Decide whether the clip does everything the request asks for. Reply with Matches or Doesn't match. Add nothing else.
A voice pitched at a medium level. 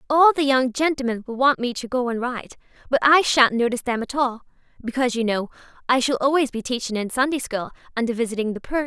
Doesn't match